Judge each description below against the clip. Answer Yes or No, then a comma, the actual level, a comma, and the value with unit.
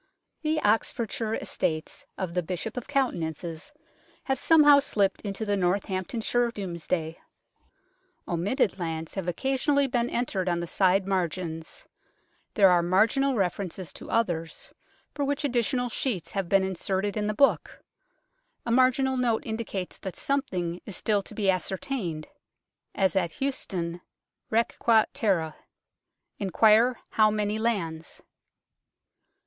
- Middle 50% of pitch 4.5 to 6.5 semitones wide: Yes, average, 5.1 semitones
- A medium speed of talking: No, slow, 130 wpm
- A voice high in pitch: Yes, high, 200 Hz